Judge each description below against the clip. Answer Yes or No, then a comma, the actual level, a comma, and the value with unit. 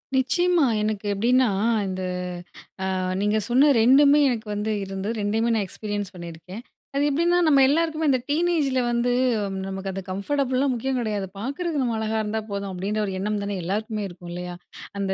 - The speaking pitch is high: Yes, high, 220 Hz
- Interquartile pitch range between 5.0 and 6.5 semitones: Yes, wide, 5.6 semitones